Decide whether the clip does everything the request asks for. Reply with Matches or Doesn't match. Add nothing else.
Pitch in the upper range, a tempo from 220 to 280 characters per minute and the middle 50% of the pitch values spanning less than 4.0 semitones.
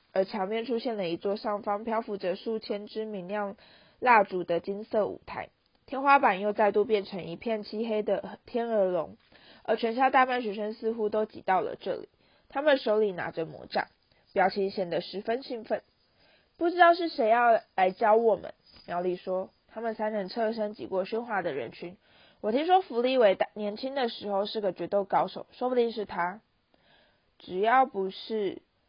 Matches